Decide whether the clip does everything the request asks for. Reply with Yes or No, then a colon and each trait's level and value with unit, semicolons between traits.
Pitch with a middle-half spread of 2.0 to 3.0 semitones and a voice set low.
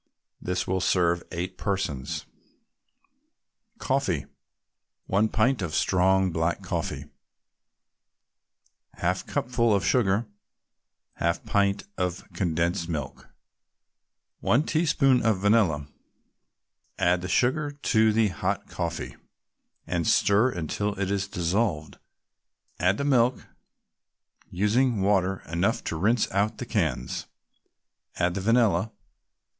No: average, 4.3 semitones; low, 100 Hz